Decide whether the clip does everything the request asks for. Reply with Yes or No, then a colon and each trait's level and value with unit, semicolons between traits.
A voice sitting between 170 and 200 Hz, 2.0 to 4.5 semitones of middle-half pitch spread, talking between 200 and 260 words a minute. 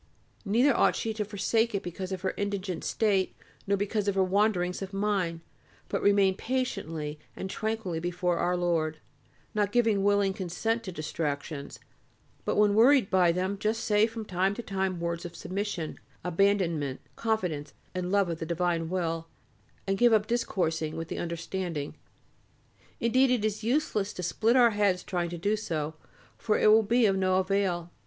No: high, 190 Hz; average, 3.5 semitones; average, 170 wpm